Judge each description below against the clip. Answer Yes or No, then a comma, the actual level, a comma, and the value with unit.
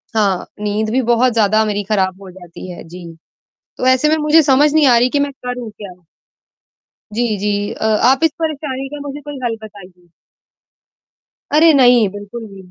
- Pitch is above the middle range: Yes, high, 235 Hz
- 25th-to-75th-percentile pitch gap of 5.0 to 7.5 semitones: Yes, wide, 5.6 semitones